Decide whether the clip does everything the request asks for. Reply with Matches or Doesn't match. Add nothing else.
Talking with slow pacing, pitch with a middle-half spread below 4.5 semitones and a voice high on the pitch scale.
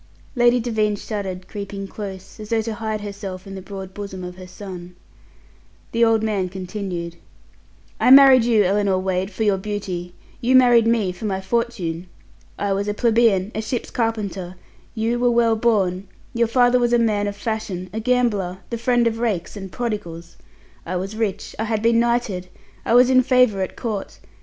Doesn't match